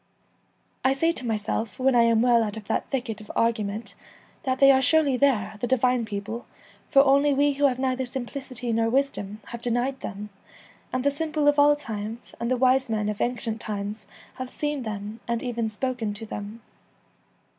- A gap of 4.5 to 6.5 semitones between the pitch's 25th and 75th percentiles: No, average, 3.5 semitones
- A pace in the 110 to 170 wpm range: No, average, 190 wpm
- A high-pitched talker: Yes, high, 245 Hz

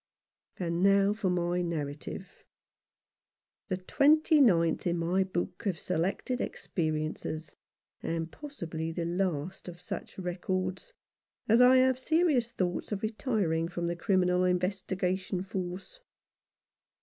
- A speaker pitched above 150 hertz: Yes, medium, 185 Hz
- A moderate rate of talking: No, slow, 120 wpm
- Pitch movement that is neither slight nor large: Yes, average, 3.4 semitones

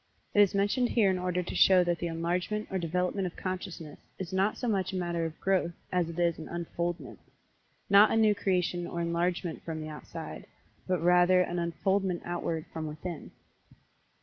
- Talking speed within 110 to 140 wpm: No, average, 180 wpm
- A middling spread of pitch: No, narrow, 2.0 semitones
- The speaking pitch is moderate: Yes, medium, 180 Hz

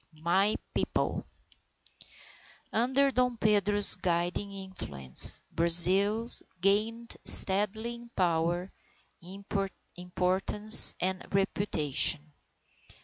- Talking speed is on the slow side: Yes, slow, 75 wpm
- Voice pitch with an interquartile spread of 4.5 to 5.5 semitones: No, average, 3.6 semitones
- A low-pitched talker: No, high, 195 Hz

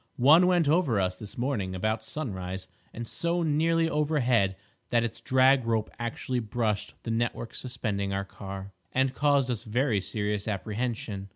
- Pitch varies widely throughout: No, average, 5.0 semitones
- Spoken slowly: No, average, 155 wpm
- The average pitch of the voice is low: Yes, low, 115 Hz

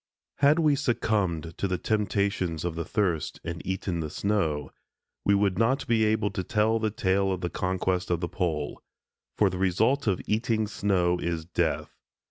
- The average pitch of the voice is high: No, very low, 95 Hz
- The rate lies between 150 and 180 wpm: Yes, average, 175 wpm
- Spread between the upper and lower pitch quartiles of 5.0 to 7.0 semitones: No, average, 3.7 semitones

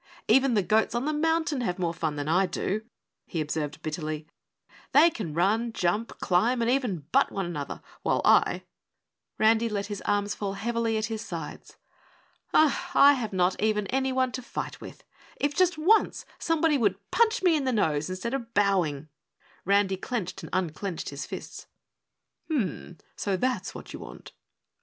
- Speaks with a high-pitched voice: Yes, high, 210 Hz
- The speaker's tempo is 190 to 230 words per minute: No, average, 170 wpm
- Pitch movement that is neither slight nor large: No, wide, 6.0 semitones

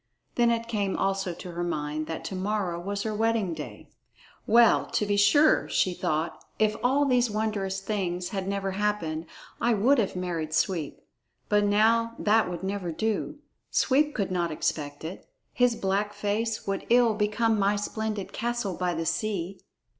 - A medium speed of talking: Yes, average, 170 wpm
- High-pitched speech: Yes, high, 205 Hz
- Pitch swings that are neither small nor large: Yes, average, 3.5 semitones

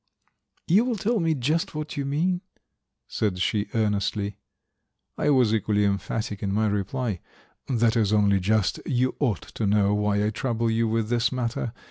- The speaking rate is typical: Yes, average, 165 wpm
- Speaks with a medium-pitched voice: No, low, 110 Hz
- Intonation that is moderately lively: Yes, average, 4.0 semitones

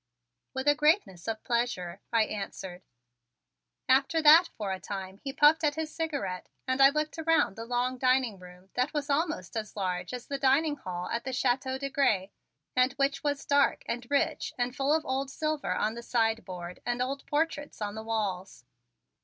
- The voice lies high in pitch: Yes, very high, 255 Hz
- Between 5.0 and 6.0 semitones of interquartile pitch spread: Yes, wide, 5.5 semitones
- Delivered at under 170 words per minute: No, average, 185 wpm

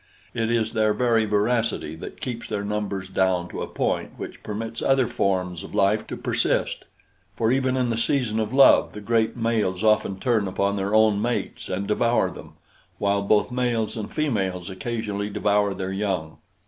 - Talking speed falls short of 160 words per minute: No, average, 175 wpm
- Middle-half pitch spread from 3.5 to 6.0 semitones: No, average, 2.8 semitones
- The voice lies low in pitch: Yes, low, 105 Hz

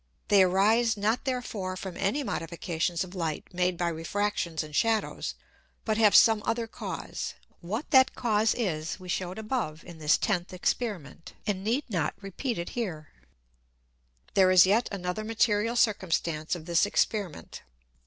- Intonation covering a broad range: No, average, 4.2 semitones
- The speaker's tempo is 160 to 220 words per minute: No, average, 150 wpm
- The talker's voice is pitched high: Yes, high, 195 Hz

